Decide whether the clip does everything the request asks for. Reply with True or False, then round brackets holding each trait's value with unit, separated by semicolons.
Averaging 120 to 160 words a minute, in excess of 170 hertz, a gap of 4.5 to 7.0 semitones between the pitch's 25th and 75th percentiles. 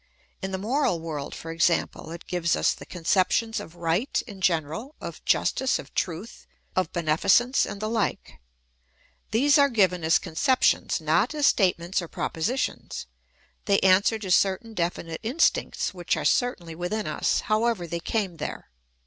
True (155 wpm; 185 Hz; 5.0 semitones)